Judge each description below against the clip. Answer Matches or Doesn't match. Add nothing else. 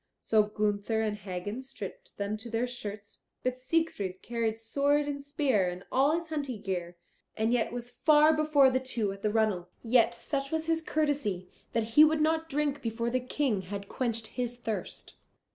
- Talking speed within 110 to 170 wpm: Doesn't match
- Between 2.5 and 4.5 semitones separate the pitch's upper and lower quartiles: Doesn't match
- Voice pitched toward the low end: Doesn't match